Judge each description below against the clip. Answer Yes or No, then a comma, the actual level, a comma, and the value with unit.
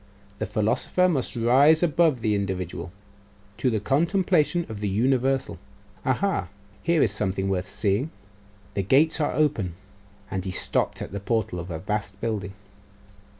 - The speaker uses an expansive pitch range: Yes, wide, 6.9 semitones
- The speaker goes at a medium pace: Yes, average, 150 wpm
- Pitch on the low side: Yes, low, 110 Hz